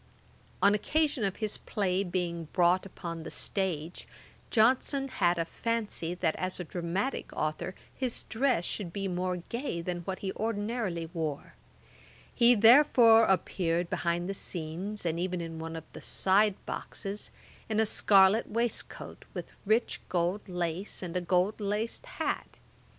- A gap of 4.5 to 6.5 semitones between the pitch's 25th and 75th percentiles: No, average, 4.0 semitones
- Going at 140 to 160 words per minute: Yes, average, 150 wpm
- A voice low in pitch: No, high, 190 Hz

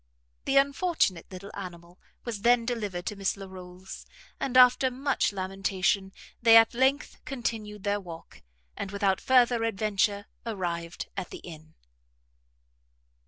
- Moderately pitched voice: No, high, 205 Hz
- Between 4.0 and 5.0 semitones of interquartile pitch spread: Yes, average, 4.5 semitones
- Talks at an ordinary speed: No, slow, 125 wpm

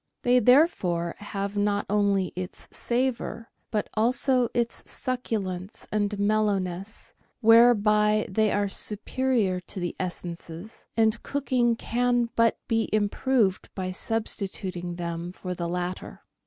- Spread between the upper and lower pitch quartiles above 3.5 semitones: Yes, average, 3.9 semitones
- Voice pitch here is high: Yes, high, 210 Hz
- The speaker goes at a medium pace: No, slow, 115 wpm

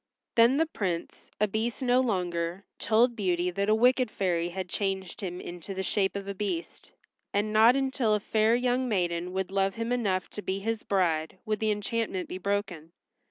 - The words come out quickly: No, average, 190 wpm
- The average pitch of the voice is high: Yes, high, 200 Hz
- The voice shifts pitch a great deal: No, average, 3.6 semitones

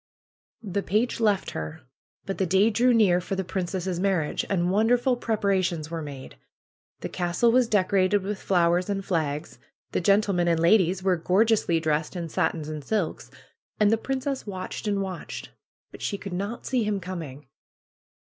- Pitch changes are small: No, average, 3.4 semitones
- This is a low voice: No, high, 190 Hz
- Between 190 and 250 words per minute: No, average, 170 wpm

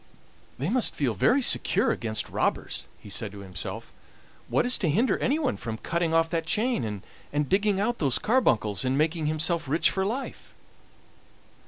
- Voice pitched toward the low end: No, medium, 165 Hz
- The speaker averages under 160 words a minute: No, average, 165 wpm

